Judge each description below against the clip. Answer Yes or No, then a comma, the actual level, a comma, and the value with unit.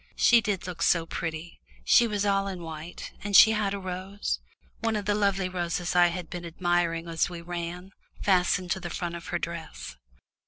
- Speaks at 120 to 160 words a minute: No, average, 195 wpm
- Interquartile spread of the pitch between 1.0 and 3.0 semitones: Yes, narrow, 2.6 semitones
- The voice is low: No, medium, 180 Hz